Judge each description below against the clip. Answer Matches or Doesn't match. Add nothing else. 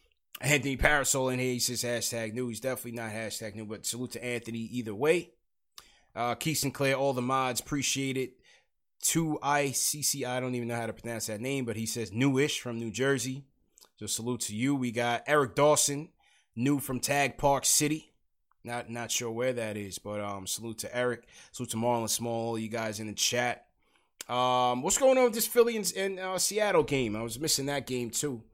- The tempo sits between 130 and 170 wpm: Doesn't match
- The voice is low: Matches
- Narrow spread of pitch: Doesn't match